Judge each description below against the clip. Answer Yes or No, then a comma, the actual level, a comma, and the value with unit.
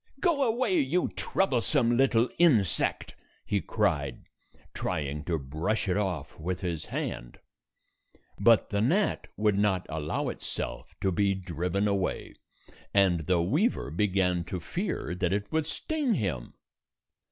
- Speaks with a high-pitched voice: No, low, 100 Hz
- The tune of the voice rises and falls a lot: Yes, wide, 7.3 semitones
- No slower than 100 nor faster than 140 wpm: Yes, slow, 135 wpm